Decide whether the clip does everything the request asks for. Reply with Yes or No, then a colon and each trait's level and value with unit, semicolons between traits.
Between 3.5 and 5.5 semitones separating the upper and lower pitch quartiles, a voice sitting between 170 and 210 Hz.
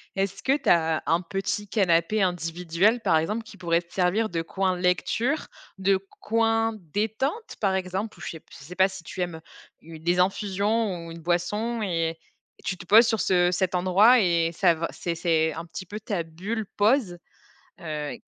Yes: average, 3.9 semitones; medium, 185 Hz